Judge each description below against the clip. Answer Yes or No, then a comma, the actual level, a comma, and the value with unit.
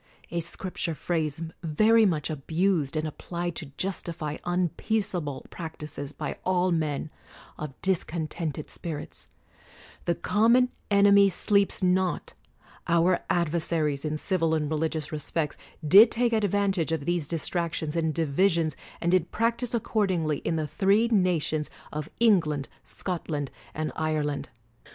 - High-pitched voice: No, medium, 170 Hz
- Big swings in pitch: No, average, 3.6 semitones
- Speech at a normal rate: No, slow, 130 wpm